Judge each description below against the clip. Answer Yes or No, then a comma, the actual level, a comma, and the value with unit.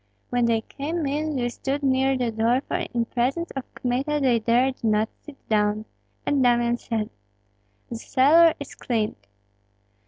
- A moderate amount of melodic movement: Yes, average, 3.1 semitones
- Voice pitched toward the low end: No, very high, 250 Hz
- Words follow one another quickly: No, average, 155 wpm